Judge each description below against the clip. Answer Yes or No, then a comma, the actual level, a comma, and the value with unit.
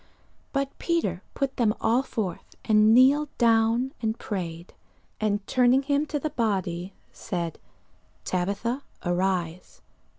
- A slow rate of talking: Yes, slow, 120 wpm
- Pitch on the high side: Yes, high, 220 Hz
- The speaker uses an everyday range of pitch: No, wide, 6.0 semitones